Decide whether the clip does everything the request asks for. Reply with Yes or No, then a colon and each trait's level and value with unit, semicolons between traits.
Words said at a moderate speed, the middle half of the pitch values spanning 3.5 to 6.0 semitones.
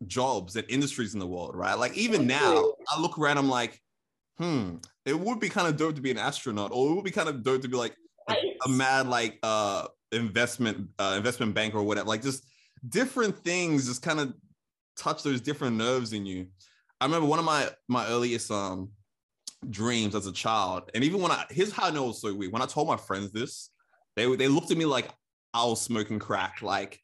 No: fast, 215 wpm; average, 5.2 semitones